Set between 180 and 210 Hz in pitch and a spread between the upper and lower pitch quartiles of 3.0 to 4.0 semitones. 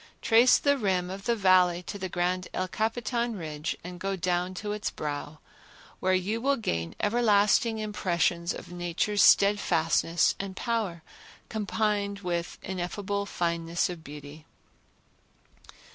Yes: medium, 185 Hz; average, 3.3 semitones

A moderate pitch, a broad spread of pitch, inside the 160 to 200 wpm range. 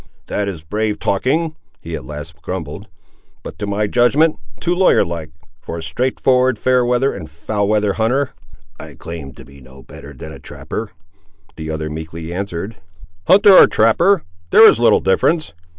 No: low, 100 Hz; wide, 7.8 semitones; average, 165 wpm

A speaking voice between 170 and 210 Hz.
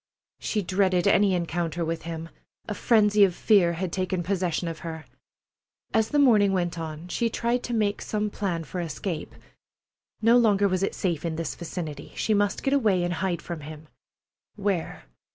Yes: medium, 185 Hz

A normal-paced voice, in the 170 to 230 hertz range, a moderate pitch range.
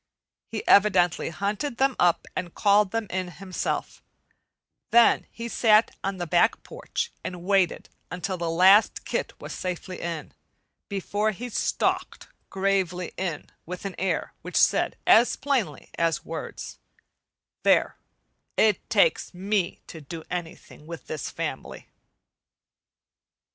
No: slow, 125 wpm; high, 190 Hz; average, 3.4 semitones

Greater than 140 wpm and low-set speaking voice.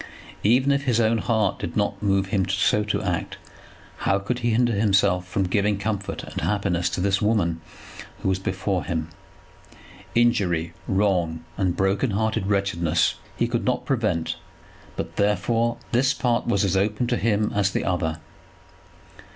Yes: average, 160 wpm; low, 100 Hz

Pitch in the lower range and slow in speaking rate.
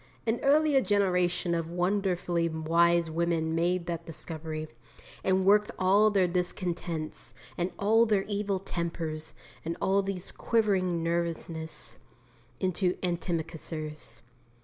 No: medium, 175 Hz; slow, 110 wpm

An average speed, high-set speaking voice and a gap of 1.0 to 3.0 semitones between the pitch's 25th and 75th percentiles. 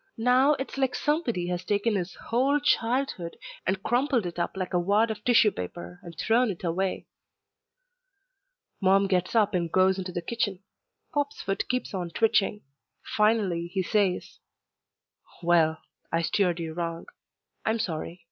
No: average, 150 wpm; high, 195 Hz; average, 4.7 semitones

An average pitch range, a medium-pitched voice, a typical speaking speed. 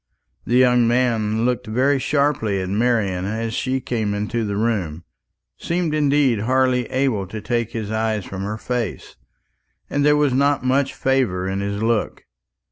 No: average, 3.8 semitones; low, 115 Hz; average, 160 wpm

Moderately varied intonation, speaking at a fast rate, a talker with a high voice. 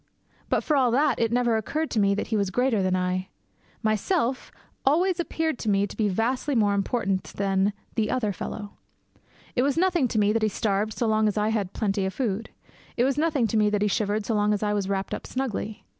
Yes: average, 3.8 semitones; fast, 230 wpm; high, 215 Hz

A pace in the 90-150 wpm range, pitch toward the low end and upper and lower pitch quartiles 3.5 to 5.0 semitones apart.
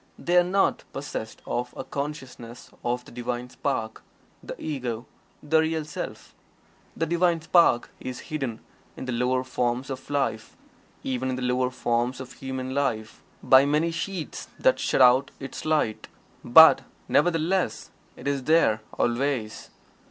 Yes: average, 145 wpm; low, 130 Hz; average, 4.0 semitones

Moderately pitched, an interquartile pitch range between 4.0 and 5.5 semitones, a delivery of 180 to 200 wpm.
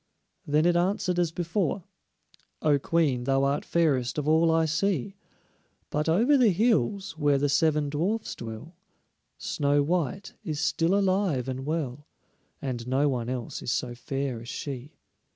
No: medium, 150 Hz; average, 4.5 semitones; average, 150 wpm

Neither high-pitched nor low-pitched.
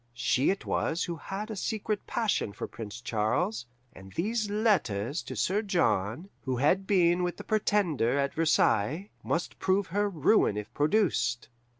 Yes: medium, 170 Hz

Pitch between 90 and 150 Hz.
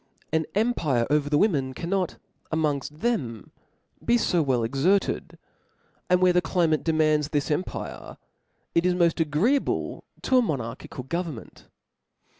No: medium, 160 Hz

